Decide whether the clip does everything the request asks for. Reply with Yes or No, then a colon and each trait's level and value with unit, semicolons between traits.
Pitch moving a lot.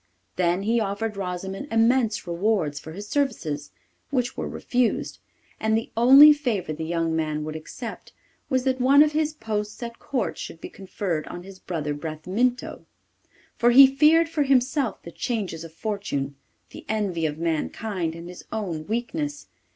Yes: wide, 6.9 semitones